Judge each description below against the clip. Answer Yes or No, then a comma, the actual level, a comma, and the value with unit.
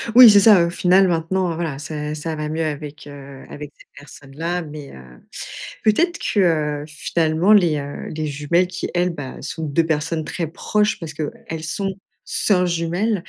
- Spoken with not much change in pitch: No, average, 3.3 semitones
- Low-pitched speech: No, medium, 160 Hz